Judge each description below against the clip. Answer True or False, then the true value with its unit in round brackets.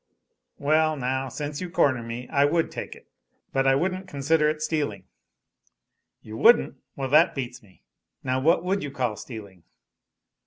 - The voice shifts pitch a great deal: False (4.0 semitones)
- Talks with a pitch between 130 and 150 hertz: True (140 Hz)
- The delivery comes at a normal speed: True (160 wpm)